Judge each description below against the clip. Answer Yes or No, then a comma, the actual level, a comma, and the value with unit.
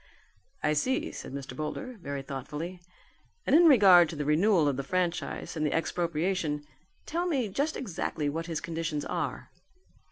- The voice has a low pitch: No, medium, 165 Hz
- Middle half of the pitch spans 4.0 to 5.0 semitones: Yes, average, 4.7 semitones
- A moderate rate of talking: Yes, average, 160 wpm